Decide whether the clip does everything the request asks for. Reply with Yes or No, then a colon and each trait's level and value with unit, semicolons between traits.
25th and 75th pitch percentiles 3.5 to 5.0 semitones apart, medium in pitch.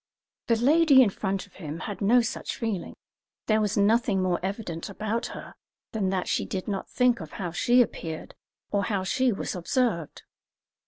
No: average, 3.8 semitones; high, 205 Hz